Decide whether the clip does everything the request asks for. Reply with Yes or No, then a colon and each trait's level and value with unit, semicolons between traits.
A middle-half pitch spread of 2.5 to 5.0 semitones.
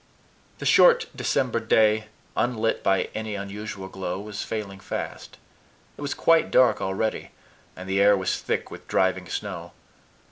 Yes: average, 2.8 semitones